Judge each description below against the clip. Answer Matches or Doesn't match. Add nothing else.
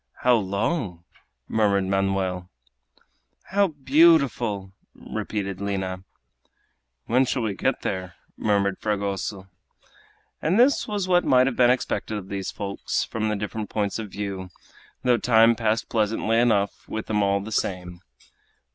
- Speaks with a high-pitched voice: Doesn't match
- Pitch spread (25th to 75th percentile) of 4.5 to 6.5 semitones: Doesn't match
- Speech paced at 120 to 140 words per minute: Matches